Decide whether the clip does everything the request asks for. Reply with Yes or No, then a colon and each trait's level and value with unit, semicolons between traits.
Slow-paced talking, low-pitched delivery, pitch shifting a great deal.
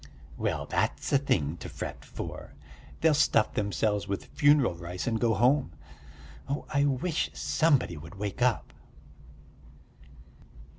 Yes: slow, 130 wpm; low, 115 Hz; wide, 6.5 semitones